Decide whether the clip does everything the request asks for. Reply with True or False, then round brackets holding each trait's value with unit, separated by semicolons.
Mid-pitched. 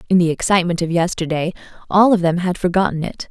True (175 Hz)